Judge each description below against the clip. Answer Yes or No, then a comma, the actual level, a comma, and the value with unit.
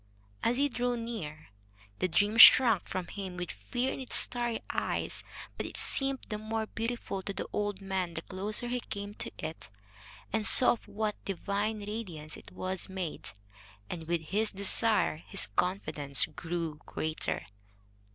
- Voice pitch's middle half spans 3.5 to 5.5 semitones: Yes, average, 4.2 semitones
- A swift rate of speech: No, average, 160 wpm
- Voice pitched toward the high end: Yes, high, 200 Hz